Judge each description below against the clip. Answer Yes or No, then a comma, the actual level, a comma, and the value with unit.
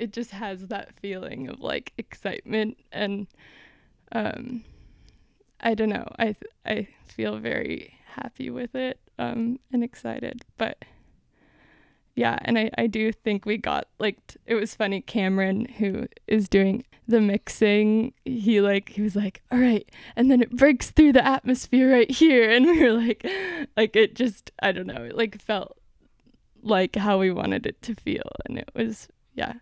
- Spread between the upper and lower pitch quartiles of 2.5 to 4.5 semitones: Yes, average, 2.9 semitones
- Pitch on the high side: Yes, high, 225 Hz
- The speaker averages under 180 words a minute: Yes, average, 170 wpm